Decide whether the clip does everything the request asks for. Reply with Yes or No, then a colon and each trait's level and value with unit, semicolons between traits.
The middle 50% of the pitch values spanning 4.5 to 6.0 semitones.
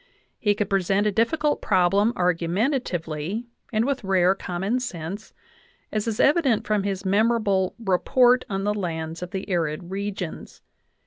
No: average, 3.8 semitones